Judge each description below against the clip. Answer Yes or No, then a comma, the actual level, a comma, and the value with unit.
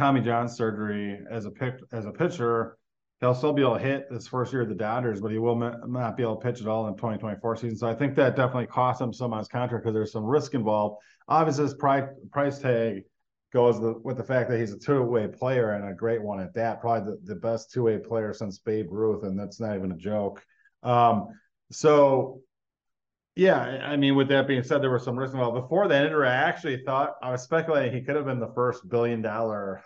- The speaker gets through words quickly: Yes, fast, 245 wpm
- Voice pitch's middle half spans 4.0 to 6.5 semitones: No, average, 3.0 semitones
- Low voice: Yes, low, 120 Hz